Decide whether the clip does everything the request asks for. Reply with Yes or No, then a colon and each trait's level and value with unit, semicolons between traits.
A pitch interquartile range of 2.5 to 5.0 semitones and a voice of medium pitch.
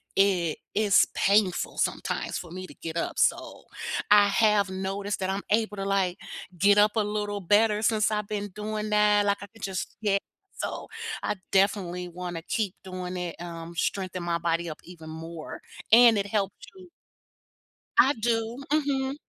No: average, 2.8 semitones; high, 200 Hz